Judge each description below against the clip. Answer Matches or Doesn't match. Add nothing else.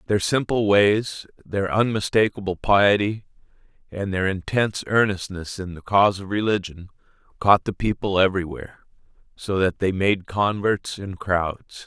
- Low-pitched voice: Matches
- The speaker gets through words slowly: Matches